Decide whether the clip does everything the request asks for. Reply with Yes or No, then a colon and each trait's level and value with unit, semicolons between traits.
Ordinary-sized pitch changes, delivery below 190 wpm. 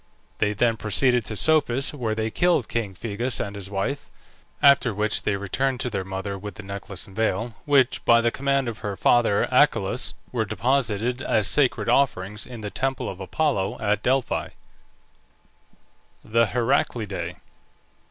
Yes: average, 4.1 semitones; average, 155 wpm